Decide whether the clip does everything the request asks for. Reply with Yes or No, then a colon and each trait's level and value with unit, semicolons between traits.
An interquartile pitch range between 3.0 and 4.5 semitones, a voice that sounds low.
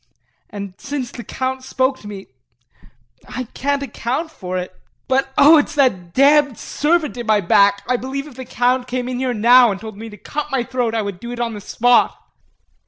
No: average, 3.8 semitones; high, 245 Hz